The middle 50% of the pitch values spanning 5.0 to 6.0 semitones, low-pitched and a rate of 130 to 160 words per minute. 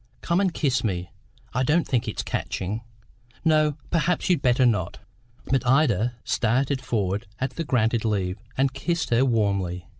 Yes: wide, 5.5 semitones; low, 125 Hz; average, 155 wpm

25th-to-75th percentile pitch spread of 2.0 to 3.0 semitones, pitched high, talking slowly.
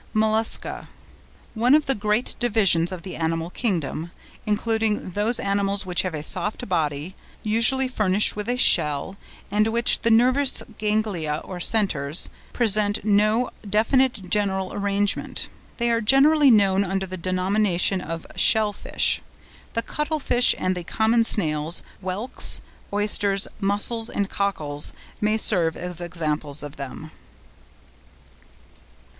No: average, 3.8 semitones; high, 205 Hz; slow, 125 wpm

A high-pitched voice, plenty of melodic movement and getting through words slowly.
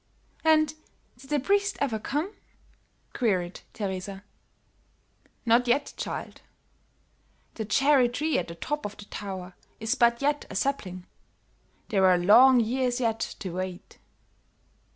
Yes: high, 235 Hz; wide, 6.3 semitones; slow, 130 wpm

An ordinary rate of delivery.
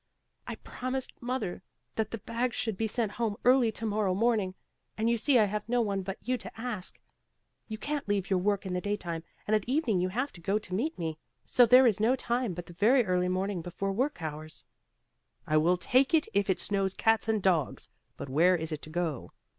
No: fast, 220 wpm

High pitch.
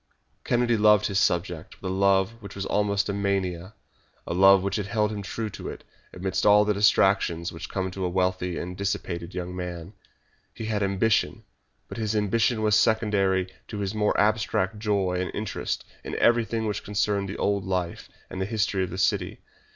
No: low, 100 Hz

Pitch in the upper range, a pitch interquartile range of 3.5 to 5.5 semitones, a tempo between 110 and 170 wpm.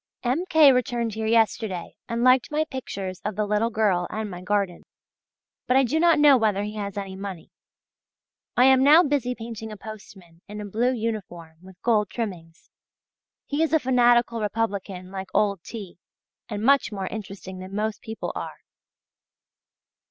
Yes: high, 215 Hz; average, 4.0 semitones; average, 165 wpm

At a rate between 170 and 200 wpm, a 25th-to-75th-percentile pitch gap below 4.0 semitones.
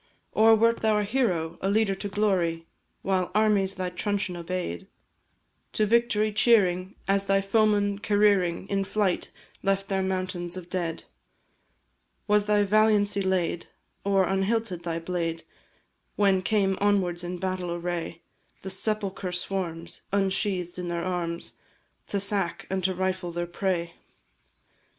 No: slow, 135 wpm; narrow, 2.5 semitones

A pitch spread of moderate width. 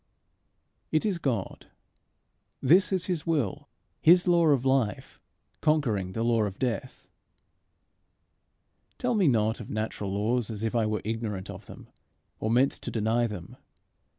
No: wide, 6.2 semitones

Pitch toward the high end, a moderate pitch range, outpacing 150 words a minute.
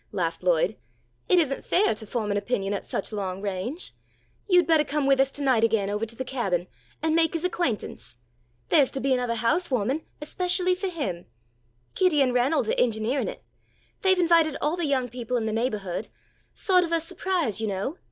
No: very high, 260 Hz; wide, 7.3 semitones; average, 190 wpm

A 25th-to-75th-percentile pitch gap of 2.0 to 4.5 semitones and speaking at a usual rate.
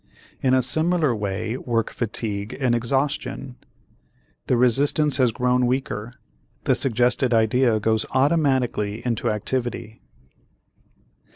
No: average, 2.8 semitones; slow, 105 wpm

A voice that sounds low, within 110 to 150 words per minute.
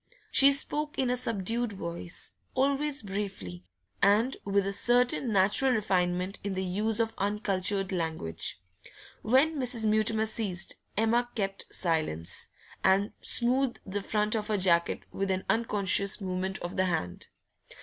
No: high, 205 Hz; average, 140 wpm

